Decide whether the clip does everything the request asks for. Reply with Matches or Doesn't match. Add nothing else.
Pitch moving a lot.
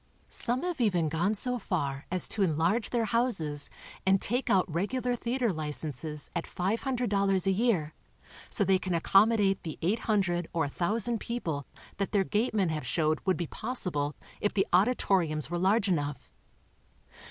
Matches